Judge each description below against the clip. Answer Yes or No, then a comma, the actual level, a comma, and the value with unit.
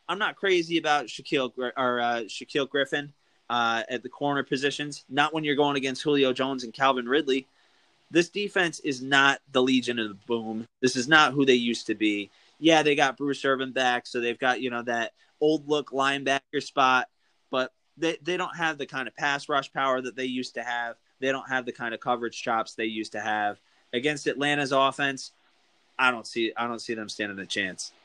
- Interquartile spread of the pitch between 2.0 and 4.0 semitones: Yes, average, 3.2 semitones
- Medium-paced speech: No, fast, 210 wpm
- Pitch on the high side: No, low, 130 Hz